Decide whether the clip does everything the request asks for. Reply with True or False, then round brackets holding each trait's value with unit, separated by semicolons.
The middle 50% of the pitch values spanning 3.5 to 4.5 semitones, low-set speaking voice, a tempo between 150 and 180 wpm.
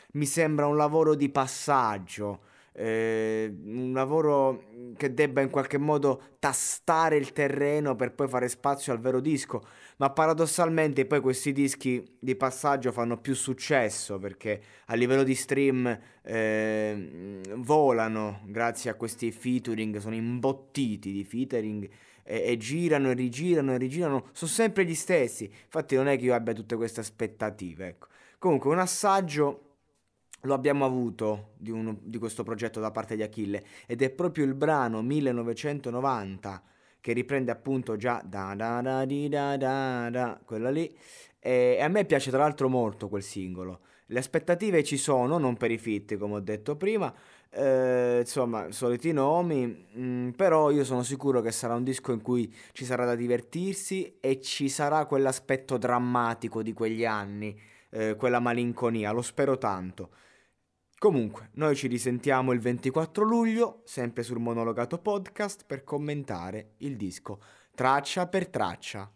True (4.0 semitones; 125 Hz; 155 wpm)